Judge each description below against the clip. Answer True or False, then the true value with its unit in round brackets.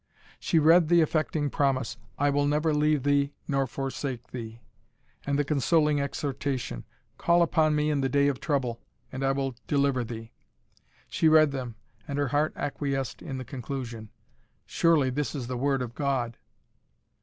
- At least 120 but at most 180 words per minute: True (165 wpm)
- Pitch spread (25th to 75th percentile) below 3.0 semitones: True (2.5 semitones)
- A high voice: False (140 Hz)